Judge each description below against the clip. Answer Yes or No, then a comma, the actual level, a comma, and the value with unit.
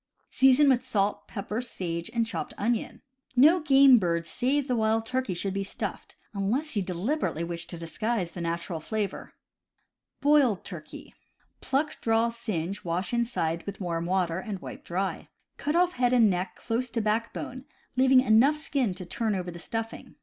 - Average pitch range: No, wide, 5.8 semitones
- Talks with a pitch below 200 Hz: No, high, 220 Hz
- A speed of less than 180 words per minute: Yes, average, 170 wpm